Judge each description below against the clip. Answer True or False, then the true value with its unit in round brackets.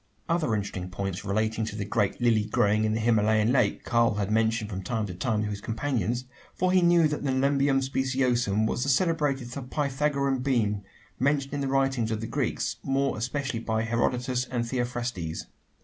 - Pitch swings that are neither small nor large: True (3.8 semitones)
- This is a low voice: True (120 Hz)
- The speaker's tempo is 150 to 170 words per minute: False (180 wpm)